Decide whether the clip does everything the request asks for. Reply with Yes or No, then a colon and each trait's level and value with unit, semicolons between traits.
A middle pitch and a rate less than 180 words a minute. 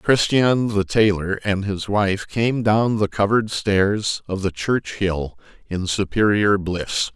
No: low, 100 Hz; average, 150 wpm